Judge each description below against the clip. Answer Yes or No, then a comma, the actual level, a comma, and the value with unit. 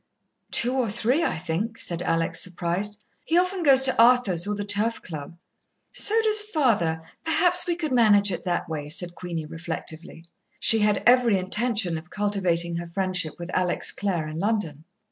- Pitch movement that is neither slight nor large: No, wide, 6.0 semitones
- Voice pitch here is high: Yes, high, 200 Hz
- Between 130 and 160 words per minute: No, average, 170 wpm